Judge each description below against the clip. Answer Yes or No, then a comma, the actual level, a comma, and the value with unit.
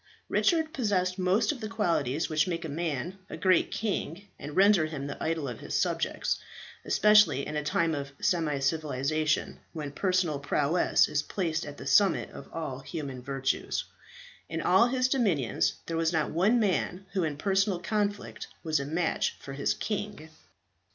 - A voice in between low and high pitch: Yes, medium, 165 Hz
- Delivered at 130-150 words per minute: No, average, 170 wpm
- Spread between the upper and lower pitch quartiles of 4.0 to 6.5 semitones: Yes, average, 5.0 semitones